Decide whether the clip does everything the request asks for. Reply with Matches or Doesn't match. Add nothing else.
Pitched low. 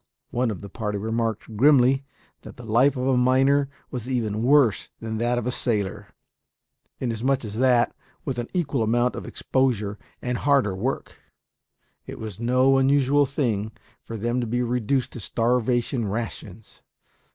Matches